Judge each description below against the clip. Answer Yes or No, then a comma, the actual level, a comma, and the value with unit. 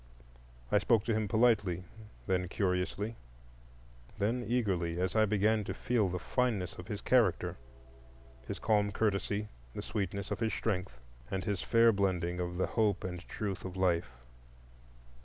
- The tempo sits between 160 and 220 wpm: No, average, 145 wpm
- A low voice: Yes, low, 100 Hz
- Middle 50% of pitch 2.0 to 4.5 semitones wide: Yes, average, 3.4 semitones